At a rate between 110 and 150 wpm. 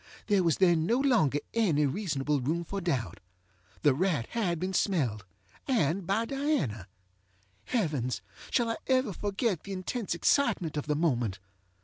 Yes: average, 140 wpm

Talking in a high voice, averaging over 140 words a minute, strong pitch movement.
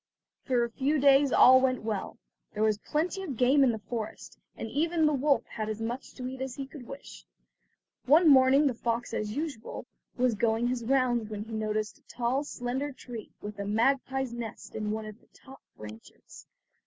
No: high, 245 Hz; average, 195 wpm; average, 3.8 semitones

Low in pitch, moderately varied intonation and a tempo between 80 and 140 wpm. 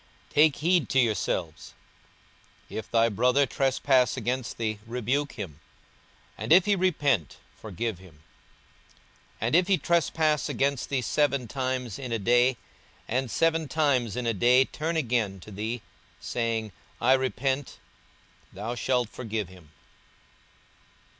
Yes: low, 125 Hz; average, 4.1 semitones; slow, 135 wpm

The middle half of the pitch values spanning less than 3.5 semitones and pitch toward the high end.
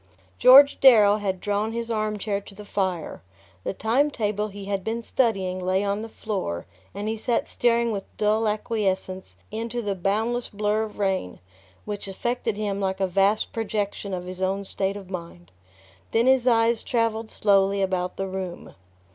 Yes: narrow, 2.6 semitones; high, 205 Hz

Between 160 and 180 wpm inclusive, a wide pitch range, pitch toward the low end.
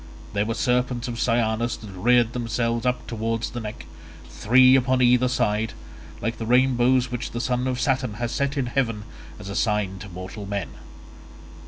No: average, 175 wpm; narrow, 2.5 semitones; low, 120 Hz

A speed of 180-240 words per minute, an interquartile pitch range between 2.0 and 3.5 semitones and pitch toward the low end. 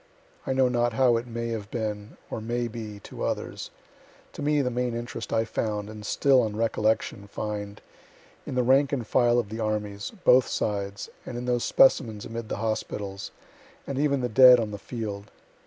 Yes: average, 190 wpm; average, 2.8 semitones; low, 115 Hz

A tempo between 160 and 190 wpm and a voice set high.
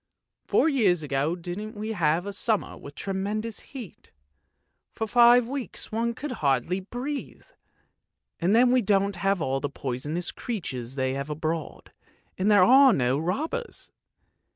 No: average, 145 wpm; high, 195 Hz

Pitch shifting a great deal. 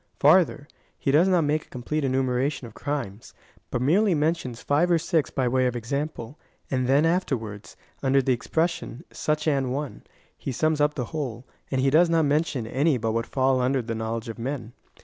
No: average, 3.8 semitones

